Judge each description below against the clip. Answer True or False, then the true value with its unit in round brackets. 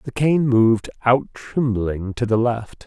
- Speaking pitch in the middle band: False (120 Hz)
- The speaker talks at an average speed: True (170 wpm)